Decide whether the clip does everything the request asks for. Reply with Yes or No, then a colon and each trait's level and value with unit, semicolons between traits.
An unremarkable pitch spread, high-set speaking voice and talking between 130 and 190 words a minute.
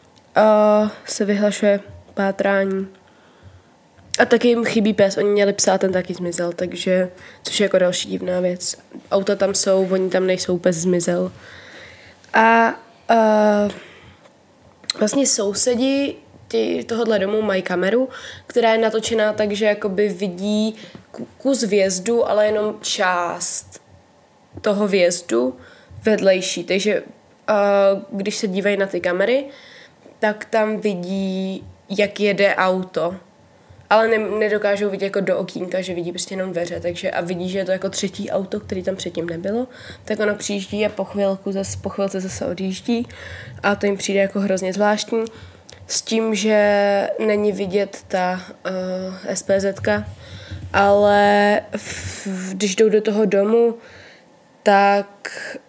No: narrow, 2.2 semitones; high, 200 Hz; average, 135 wpm